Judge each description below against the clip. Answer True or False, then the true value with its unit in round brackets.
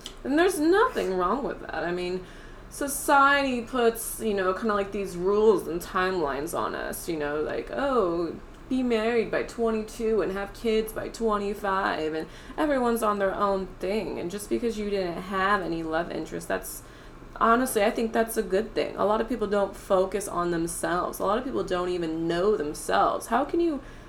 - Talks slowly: False (190 wpm)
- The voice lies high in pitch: True (205 Hz)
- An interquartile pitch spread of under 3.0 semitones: False (4.1 semitones)